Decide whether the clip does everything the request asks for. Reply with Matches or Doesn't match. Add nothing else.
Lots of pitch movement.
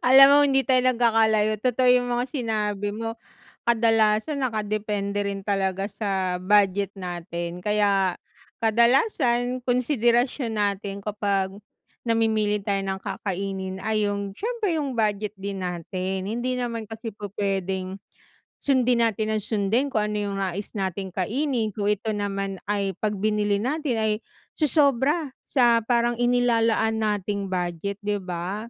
Doesn't match